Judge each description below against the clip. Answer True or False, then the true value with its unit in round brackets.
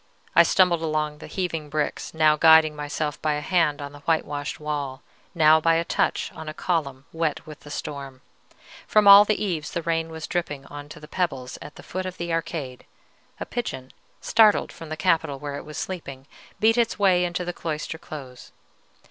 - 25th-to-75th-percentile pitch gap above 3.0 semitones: False (2.7 semitones)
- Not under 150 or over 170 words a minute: False (195 wpm)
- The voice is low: False (155 Hz)